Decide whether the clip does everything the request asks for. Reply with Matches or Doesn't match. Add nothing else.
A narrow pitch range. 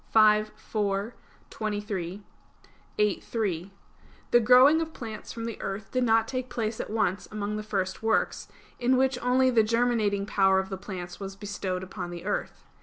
Doesn't match